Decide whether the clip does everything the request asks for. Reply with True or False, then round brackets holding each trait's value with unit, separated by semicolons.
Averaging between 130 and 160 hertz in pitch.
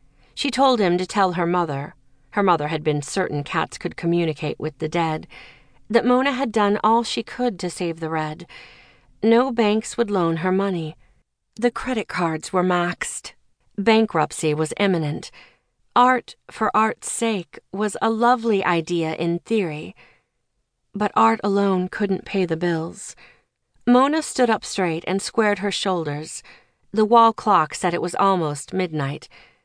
False (185 Hz)